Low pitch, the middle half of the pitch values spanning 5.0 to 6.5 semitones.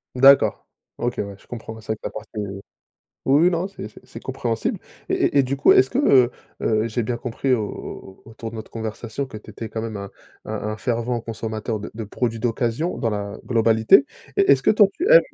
No: low, 115 Hz; average, 3.0 semitones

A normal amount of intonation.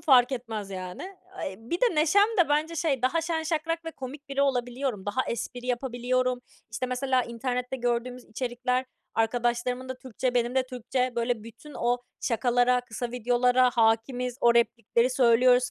No: narrow, 1.8 semitones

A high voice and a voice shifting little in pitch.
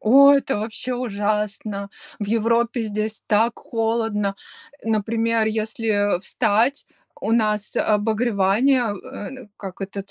Yes: high, 220 Hz; narrow, 2.0 semitones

